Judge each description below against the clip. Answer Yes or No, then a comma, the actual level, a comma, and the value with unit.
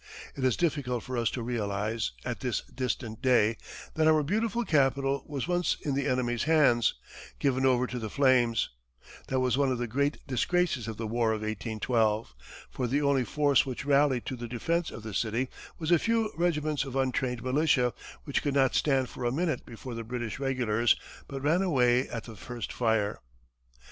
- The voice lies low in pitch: Yes, low, 130 Hz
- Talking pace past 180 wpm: Yes, average, 190 wpm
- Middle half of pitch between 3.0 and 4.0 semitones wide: Yes, average, 3.3 semitones